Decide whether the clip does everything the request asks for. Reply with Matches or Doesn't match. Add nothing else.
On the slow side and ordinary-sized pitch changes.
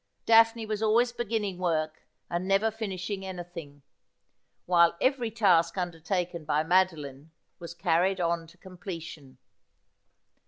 Matches